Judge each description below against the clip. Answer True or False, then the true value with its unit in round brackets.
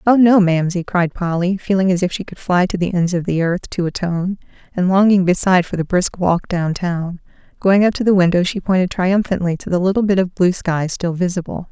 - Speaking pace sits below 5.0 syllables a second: False (5.5 syllables/s)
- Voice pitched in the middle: True (180 Hz)